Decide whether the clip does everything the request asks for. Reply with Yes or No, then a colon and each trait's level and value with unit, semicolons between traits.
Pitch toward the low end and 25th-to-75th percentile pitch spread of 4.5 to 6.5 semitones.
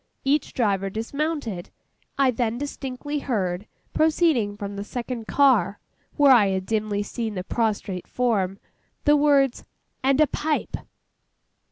No: high, 235 Hz; wide, 5.5 semitones